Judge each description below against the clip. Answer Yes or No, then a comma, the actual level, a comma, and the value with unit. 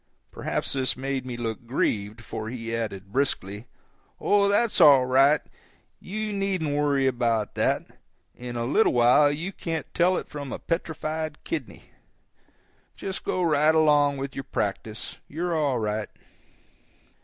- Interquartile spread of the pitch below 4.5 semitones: No, average, 5.1 semitones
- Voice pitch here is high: No, medium, 140 Hz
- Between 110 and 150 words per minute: Yes, average, 145 wpm